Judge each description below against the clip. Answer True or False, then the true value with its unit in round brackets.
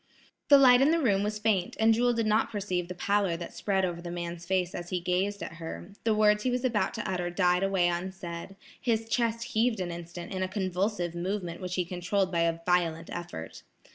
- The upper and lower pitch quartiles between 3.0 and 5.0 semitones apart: True (3.4 semitones)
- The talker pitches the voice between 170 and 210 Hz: True (185 Hz)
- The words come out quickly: True (220 wpm)